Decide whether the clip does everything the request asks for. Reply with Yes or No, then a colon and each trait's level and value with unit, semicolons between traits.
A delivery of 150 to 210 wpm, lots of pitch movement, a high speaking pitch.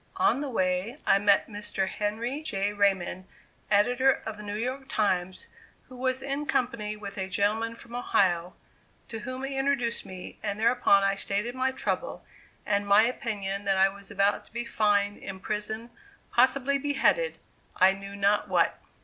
No: average, 165 wpm; average, 4.1 semitones; high, 210 Hz